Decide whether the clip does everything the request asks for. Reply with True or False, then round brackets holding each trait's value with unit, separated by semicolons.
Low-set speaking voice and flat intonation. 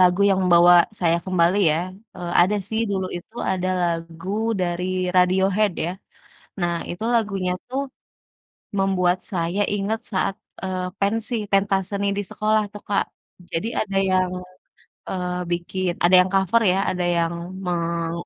False (185 Hz; 2.2 semitones)